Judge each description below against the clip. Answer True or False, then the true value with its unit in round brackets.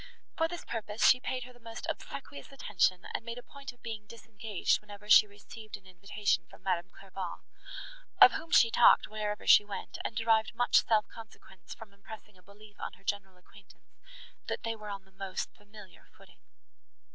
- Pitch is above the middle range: True (210 Hz)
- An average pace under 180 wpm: False (185 wpm)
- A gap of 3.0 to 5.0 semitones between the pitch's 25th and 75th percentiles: False (2.5 semitones)